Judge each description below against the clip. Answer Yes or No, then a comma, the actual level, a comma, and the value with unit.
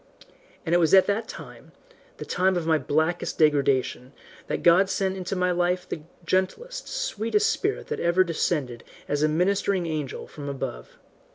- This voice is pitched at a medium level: Yes, medium, 175 Hz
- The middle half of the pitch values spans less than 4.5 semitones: Yes, average, 3.8 semitones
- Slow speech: No, average, 165 wpm